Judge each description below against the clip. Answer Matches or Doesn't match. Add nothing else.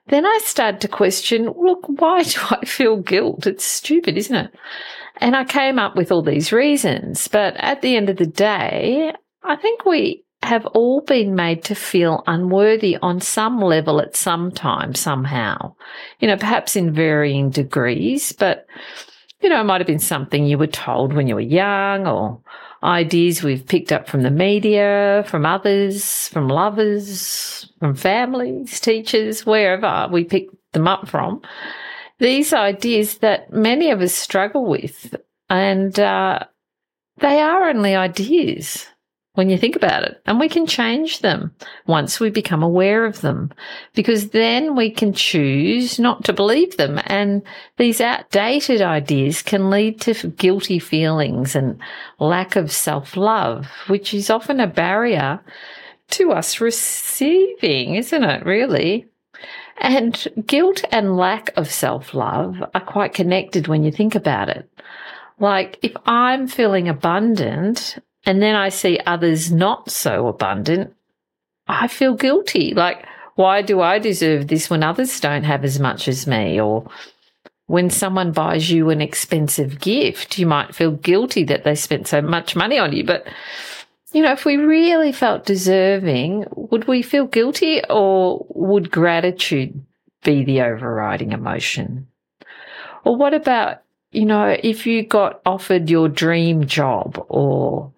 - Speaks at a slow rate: Doesn't match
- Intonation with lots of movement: Matches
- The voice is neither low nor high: Doesn't match